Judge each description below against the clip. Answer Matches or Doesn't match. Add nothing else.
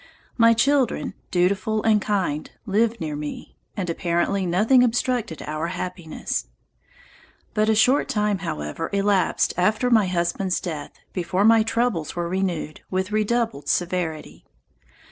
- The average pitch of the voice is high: Matches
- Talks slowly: Matches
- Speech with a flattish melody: Doesn't match